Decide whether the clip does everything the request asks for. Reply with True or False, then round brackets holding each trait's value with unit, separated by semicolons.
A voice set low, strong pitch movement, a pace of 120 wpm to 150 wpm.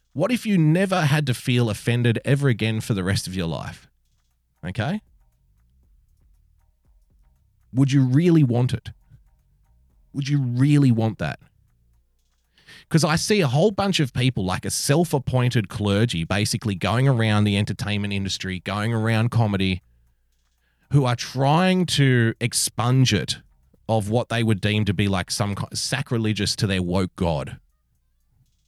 True (110 Hz; 6.2 semitones; 140 wpm)